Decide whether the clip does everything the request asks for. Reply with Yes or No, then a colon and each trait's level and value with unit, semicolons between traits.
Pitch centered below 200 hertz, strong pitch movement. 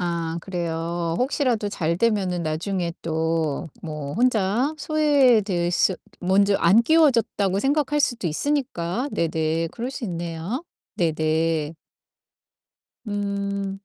Yes: high, 190 Hz; wide, 5.9 semitones